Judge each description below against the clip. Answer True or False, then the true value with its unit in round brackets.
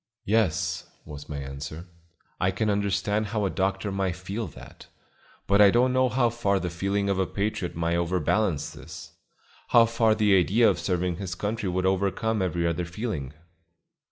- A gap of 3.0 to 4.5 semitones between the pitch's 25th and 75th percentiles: True (3.6 semitones)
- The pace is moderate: True (170 wpm)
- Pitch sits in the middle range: False (95 Hz)